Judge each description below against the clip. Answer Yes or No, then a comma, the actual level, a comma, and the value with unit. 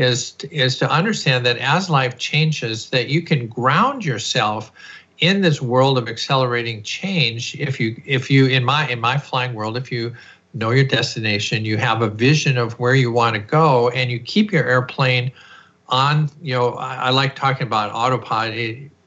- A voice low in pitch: Yes, low, 130 Hz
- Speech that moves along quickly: No, average, 180 wpm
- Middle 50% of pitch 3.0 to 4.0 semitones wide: Yes, average, 3.3 semitones